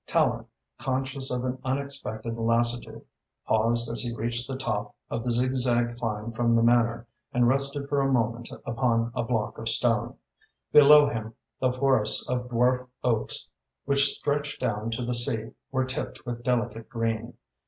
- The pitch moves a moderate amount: No, narrow, 2.1 semitones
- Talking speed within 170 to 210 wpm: No, average, 160 wpm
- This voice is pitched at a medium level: No, low, 120 Hz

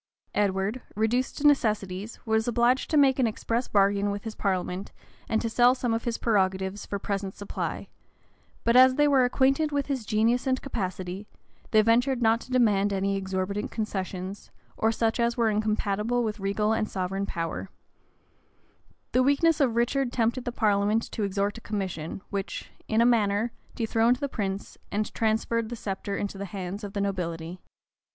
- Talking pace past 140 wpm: Yes, average, 170 wpm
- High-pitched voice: Yes, high, 215 Hz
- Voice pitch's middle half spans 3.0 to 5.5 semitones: Yes, average, 3.4 semitones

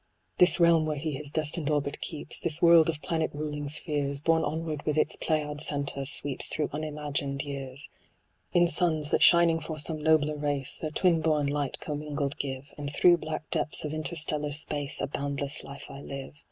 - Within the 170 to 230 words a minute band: Yes, average, 180 wpm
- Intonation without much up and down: Yes, narrow, 1.7 semitones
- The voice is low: No, medium, 150 Hz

